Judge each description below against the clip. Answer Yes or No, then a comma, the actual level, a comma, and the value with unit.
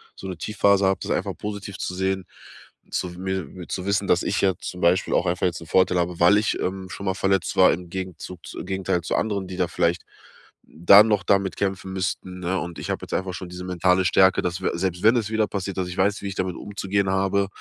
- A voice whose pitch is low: Yes, very low, 95 Hz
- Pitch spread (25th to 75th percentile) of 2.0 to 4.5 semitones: No, narrow, 1.5 semitones